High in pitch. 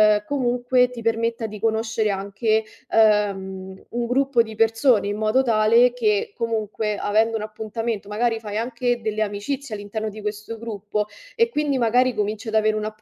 Yes: high, 220 Hz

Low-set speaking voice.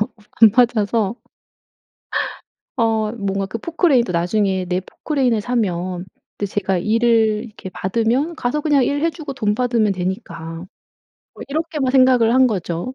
No: high, 225 Hz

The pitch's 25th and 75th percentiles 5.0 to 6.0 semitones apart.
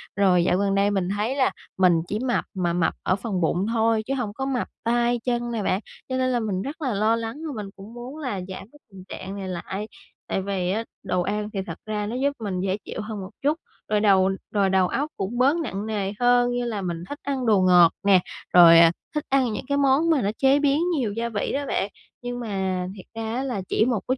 No: average, 4.5 semitones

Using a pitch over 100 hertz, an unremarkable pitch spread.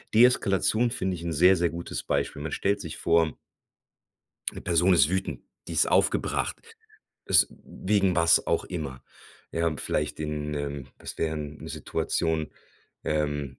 No: very low, 80 Hz; average, 3.6 semitones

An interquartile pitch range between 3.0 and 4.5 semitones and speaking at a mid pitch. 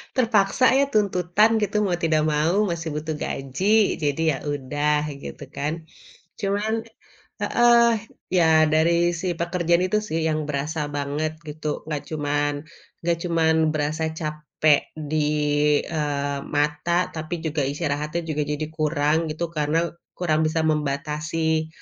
No: narrow, 2.5 semitones; medium, 155 Hz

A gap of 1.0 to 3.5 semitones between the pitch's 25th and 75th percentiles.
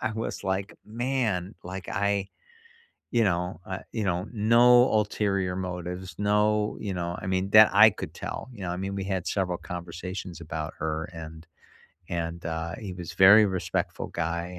Yes: average, 3.2 semitones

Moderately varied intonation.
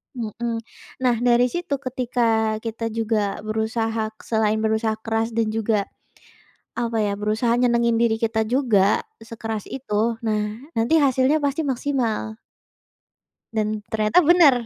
No: narrow, 2.0 semitones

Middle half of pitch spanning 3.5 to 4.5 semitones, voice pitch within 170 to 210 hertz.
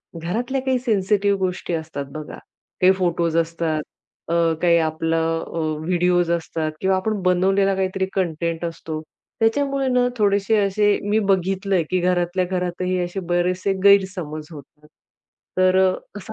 No: average, 2.8 semitones; medium, 185 Hz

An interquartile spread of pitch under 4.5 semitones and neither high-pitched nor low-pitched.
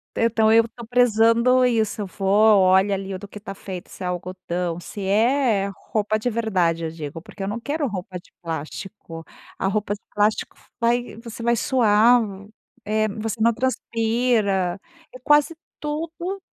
No: average, 3.6 semitones; high, 215 Hz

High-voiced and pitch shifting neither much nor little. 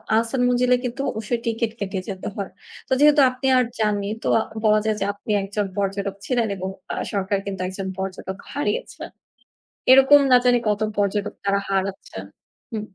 Yes: high, 210 Hz; average, 3.9 semitones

